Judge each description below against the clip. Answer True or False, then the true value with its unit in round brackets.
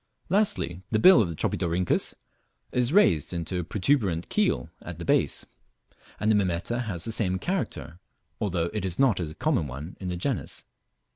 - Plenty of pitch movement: True (5.8 semitones)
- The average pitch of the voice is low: True (95 Hz)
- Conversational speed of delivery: True (170 wpm)